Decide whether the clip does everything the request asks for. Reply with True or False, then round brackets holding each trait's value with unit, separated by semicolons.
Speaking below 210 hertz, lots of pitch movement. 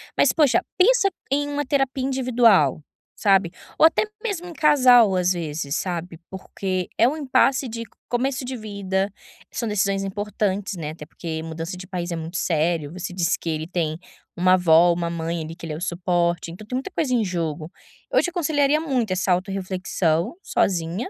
True (190 Hz; 6.8 semitones)